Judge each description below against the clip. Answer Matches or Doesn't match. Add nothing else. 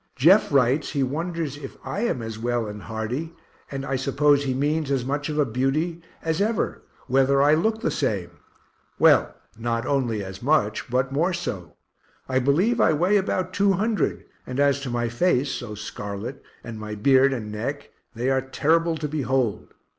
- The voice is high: Doesn't match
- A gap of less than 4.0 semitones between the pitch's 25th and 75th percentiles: Doesn't match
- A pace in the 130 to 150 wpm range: Doesn't match